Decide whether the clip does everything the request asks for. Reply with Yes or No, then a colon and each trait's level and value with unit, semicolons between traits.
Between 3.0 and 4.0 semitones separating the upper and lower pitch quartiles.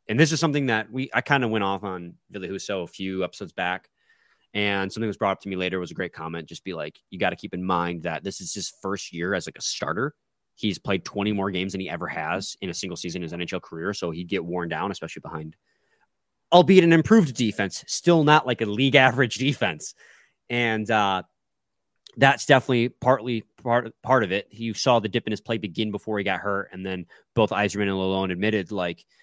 No: average, 4.9 semitones